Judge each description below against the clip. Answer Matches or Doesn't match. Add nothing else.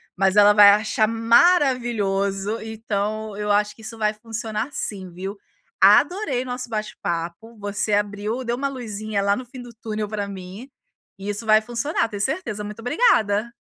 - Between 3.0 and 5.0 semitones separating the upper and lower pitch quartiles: Doesn't match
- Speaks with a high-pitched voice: Matches